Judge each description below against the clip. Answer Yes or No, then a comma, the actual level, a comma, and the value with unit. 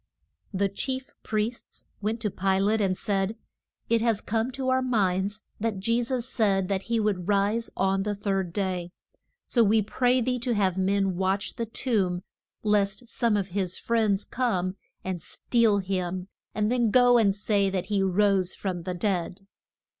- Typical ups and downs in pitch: Yes, average, 3.1 semitones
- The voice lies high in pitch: Yes, high, 205 Hz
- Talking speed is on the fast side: No, average, 170 wpm